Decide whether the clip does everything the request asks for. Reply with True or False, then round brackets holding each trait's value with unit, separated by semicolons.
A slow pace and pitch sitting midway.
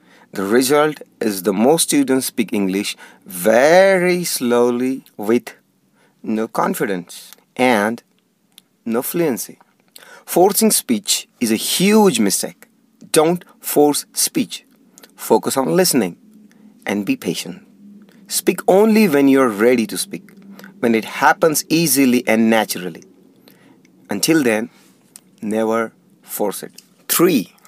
True (110 wpm; 150 Hz)